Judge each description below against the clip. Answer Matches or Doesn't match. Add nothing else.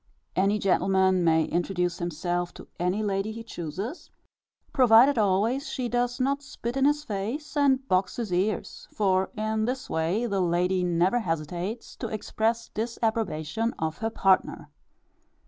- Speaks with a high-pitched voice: Matches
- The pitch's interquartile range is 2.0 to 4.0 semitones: Doesn't match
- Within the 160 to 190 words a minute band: Doesn't match